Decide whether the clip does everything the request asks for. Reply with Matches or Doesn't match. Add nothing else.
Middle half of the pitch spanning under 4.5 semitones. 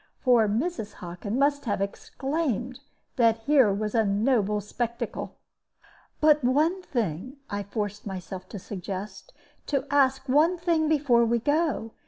Doesn't match